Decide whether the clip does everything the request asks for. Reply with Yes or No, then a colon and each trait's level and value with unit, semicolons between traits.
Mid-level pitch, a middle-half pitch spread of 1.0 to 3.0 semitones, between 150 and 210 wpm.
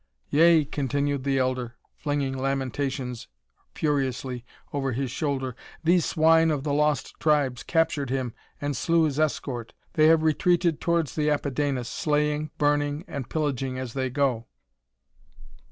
No: medium, 145 Hz; narrow, 2.6 semitones; slow, 135 wpm